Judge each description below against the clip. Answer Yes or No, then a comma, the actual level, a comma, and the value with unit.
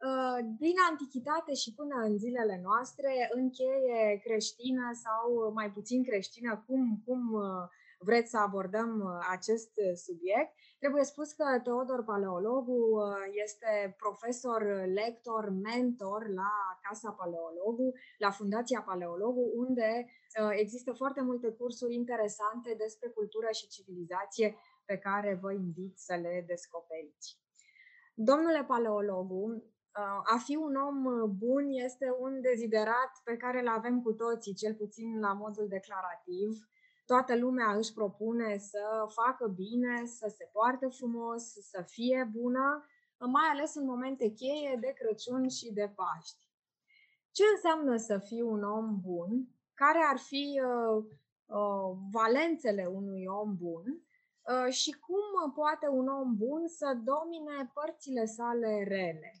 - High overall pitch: Yes, high, 230 Hz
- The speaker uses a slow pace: No, average, 125 wpm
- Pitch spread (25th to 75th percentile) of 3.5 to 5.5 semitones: Yes, average, 4.0 semitones